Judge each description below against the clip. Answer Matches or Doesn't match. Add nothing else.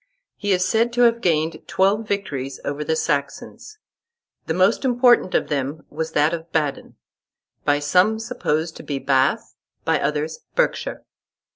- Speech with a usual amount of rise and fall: Doesn't match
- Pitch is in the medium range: Matches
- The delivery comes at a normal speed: Matches